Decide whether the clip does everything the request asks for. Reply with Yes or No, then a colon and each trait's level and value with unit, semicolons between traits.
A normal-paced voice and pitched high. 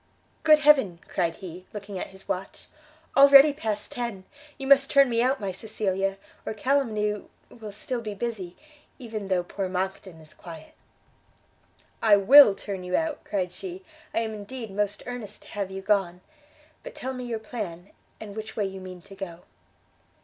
Yes: average, 170 wpm; high, 210 Hz